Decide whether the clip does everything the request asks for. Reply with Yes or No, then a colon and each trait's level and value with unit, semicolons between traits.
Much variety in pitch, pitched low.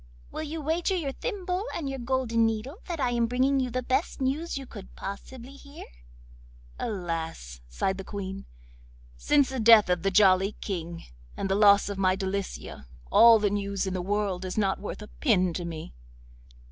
No: wide, 5.8 semitones; high, 210 Hz